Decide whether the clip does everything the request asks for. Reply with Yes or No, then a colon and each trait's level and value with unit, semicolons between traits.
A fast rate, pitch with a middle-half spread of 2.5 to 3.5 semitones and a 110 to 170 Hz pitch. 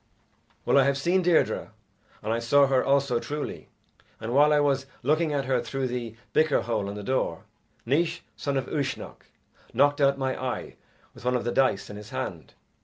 No: average, 190 wpm; average, 3.0 semitones; low, 135 Hz